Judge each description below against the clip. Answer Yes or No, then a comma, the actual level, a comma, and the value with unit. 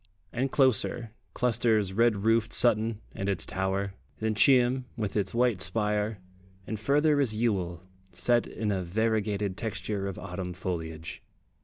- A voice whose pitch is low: Yes, low, 105 Hz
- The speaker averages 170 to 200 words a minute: No, average, 140 wpm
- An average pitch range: Yes, average, 3.3 semitones